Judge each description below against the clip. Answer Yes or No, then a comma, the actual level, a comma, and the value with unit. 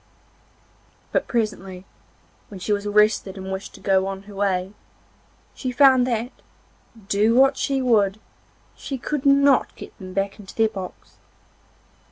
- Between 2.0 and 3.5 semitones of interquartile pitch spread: No, average, 4.4 semitones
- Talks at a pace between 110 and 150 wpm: Yes, average, 145 wpm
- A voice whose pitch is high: Yes, high, 210 Hz